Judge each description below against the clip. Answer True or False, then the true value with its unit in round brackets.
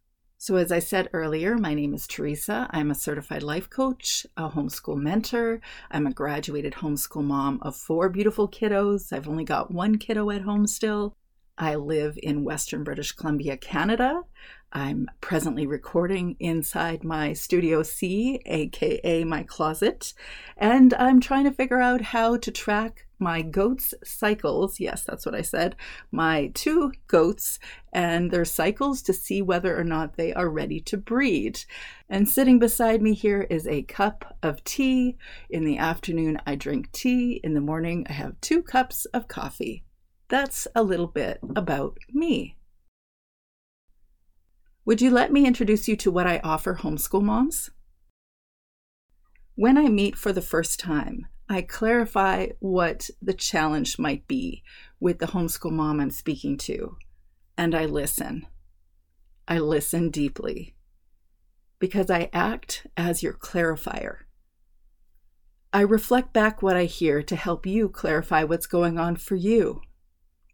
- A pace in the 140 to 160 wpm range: True (150 wpm)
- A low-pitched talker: False (175 Hz)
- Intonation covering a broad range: True (6.5 semitones)